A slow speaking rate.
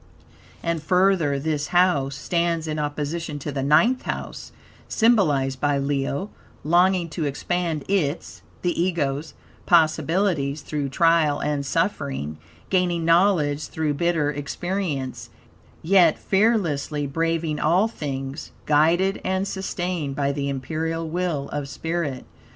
Yes: slow, 115 wpm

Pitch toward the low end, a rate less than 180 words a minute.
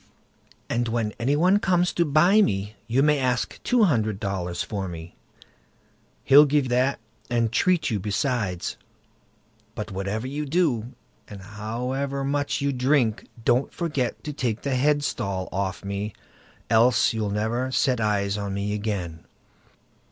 Yes: low, 120 Hz; average, 140 wpm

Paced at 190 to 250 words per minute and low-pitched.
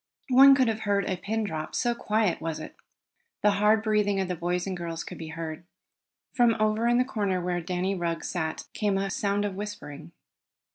No: average, 200 wpm; high, 200 Hz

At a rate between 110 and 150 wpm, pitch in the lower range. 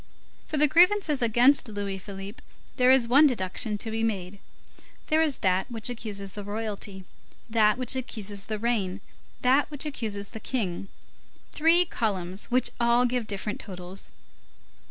No: average, 145 wpm; high, 225 Hz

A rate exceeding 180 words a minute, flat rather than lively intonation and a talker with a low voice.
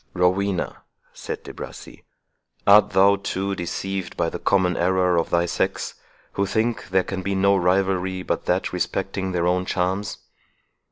No: average, 155 wpm; narrow, 1.5 semitones; very low, 95 Hz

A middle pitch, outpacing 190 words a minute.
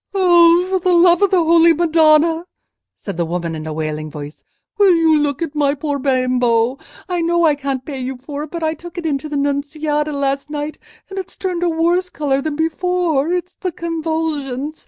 No: very high, 310 Hz; average, 200 wpm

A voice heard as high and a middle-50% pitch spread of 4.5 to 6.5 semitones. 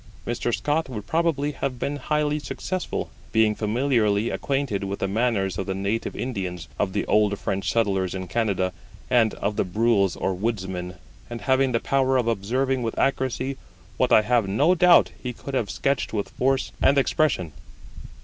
No: low, 115 Hz; average, 5.2 semitones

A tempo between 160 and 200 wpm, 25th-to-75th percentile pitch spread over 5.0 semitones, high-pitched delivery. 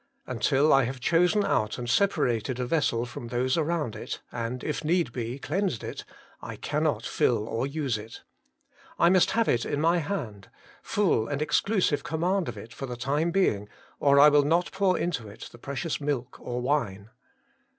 No: average, 180 wpm; wide, 5.6 semitones; medium, 140 Hz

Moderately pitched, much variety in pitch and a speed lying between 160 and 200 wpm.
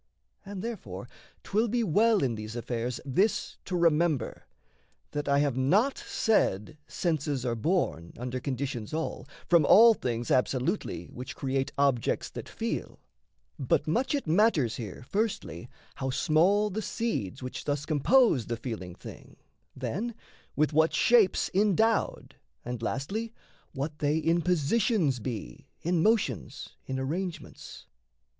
No: medium, 150 Hz; wide, 7.7 semitones; slow, 135 wpm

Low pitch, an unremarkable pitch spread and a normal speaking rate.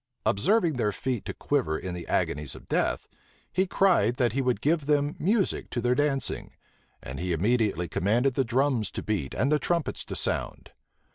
No: low, 125 Hz; wide, 6.4 semitones; average, 185 wpm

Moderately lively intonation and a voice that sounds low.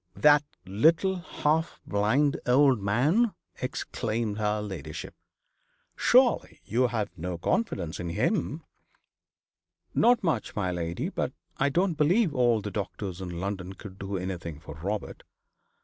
No: wide, 7.8 semitones; low, 105 Hz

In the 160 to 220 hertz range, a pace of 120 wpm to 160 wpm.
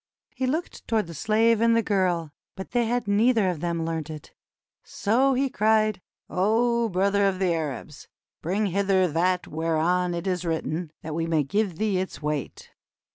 No: medium, 185 Hz; average, 175 wpm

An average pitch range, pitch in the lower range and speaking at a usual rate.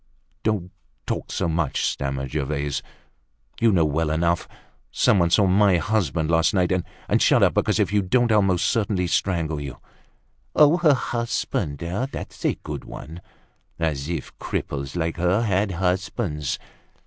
Yes: average, 4.6 semitones; very low, 90 Hz; average, 150 wpm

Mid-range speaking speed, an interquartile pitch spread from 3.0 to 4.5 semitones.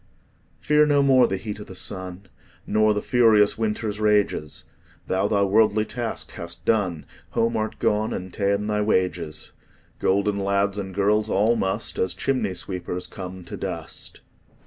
No: average, 155 wpm; narrow, 2.5 semitones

